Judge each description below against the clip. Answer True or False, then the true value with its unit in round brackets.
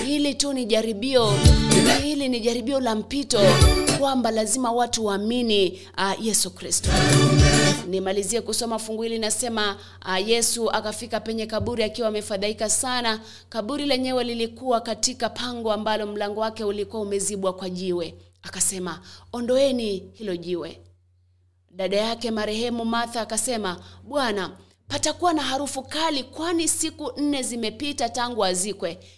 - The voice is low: False (225 Hz)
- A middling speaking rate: False (120 wpm)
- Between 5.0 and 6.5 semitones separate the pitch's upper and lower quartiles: False (3.5 semitones)